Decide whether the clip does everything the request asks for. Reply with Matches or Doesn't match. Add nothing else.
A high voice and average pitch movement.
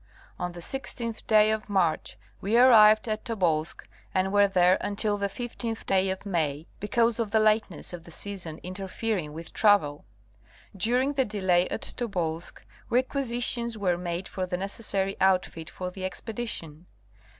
Matches